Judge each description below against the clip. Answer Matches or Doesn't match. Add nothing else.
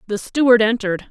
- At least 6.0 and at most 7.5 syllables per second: Matches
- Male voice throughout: Doesn't match